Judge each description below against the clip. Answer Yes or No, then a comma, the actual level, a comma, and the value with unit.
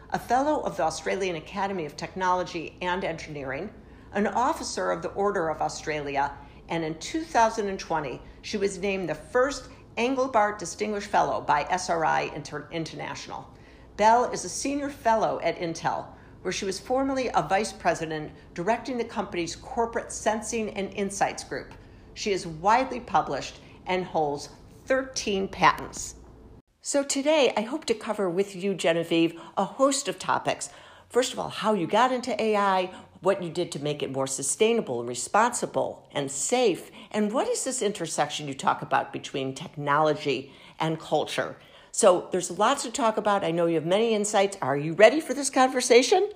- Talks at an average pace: Yes, average, 160 wpm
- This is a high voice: Yes, high, 195 Hz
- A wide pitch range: Yes, wide, 5.8 semitones